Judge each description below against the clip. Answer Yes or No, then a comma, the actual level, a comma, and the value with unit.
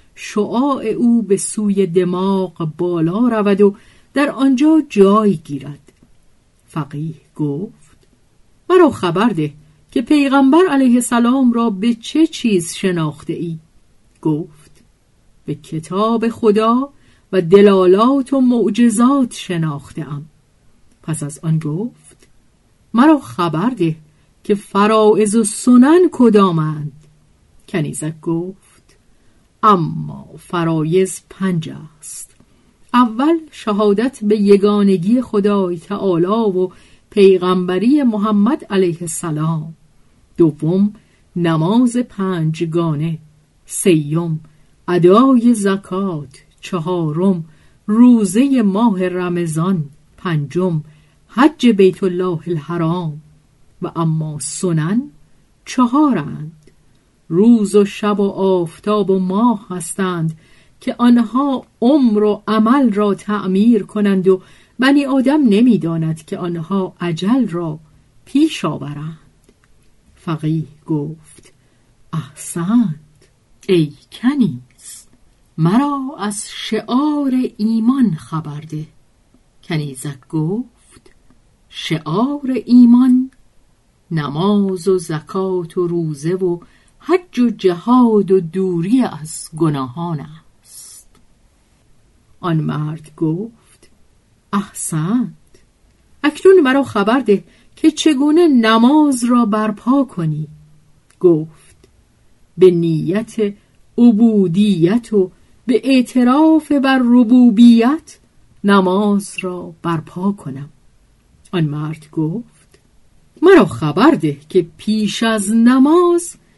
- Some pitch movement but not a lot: No, wide, 6.6 semitones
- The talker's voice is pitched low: No, high, 190 Hz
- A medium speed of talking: No, slow, 90 wpm